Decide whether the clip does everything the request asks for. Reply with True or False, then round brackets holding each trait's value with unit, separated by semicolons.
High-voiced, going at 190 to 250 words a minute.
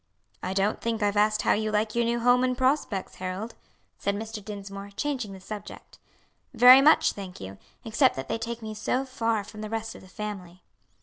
True (215 Hz; 200 wpm)